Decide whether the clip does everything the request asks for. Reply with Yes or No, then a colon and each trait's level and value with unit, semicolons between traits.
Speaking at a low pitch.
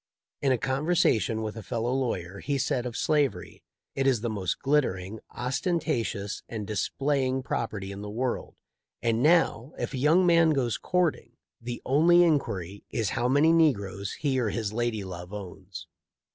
Yes: low, 120 Hz